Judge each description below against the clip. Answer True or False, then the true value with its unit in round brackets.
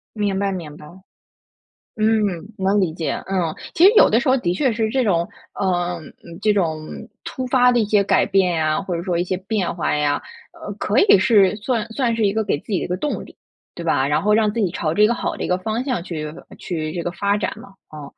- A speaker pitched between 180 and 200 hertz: True (195 Hz)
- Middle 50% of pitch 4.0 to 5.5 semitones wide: True (4.3 semitones)